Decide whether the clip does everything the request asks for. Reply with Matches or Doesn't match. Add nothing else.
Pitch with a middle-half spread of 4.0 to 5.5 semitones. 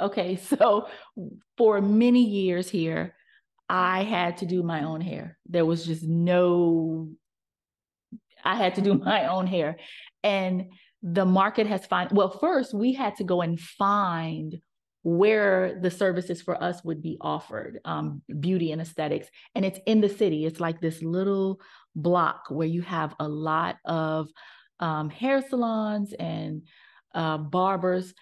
Doesn't match